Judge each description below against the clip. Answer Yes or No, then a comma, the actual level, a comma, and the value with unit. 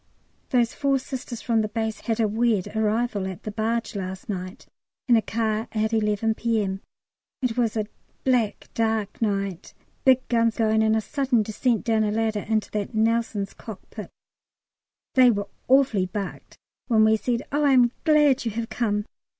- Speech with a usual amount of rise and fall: No, narrow, 2.1 semitones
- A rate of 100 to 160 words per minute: No, average, 170 wpm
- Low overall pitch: No, high, 220 Hz